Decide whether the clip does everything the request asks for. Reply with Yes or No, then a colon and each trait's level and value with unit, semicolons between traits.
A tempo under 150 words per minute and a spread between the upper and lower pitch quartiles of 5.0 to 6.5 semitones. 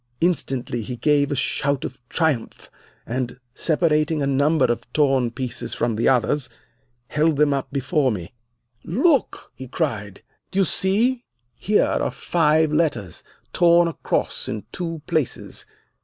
No: average, 140 wpm; average, 4.6 semitones